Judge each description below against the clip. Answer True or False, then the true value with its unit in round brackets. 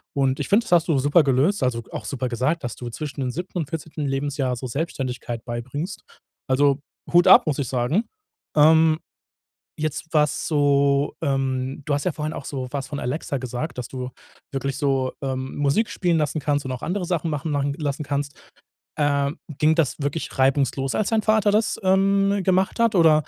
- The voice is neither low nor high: True (145 Hz)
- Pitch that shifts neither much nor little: True (3.4 semitones)